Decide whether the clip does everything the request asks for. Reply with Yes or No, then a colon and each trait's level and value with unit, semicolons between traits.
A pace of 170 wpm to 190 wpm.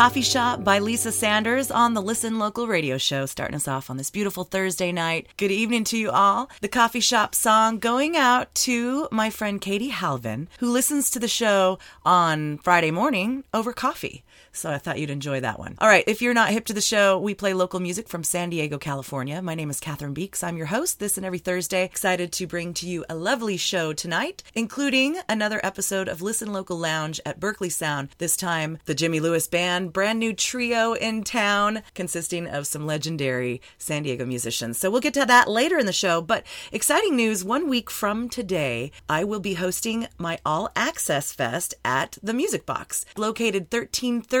No: average, 200 wpm